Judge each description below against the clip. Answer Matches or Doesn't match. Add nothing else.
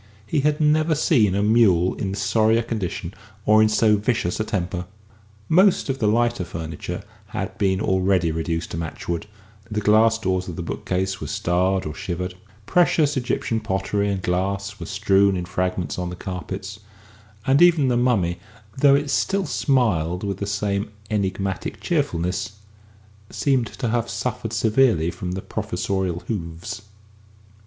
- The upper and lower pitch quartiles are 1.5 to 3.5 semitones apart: Doesn't match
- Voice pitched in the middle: Doesn't match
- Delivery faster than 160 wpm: Doesn't match